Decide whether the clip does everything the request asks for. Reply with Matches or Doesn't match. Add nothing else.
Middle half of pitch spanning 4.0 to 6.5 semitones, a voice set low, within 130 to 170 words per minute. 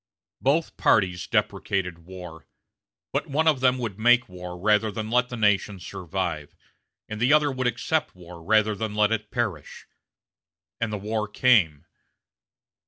Matches